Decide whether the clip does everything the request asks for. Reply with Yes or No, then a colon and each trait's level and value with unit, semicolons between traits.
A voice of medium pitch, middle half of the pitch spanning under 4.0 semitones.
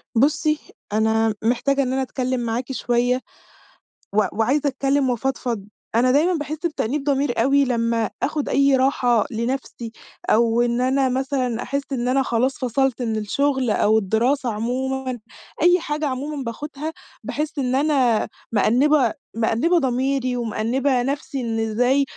No: very high, 255 Hz; average, 3.0 semitones